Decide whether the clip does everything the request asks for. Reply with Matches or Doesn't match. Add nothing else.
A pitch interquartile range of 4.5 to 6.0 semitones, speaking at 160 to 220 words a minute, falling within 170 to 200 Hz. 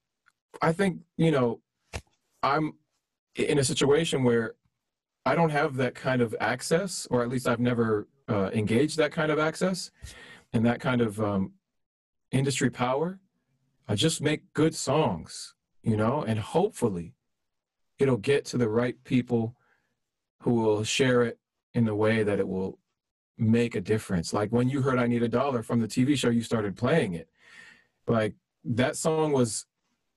Doesn't match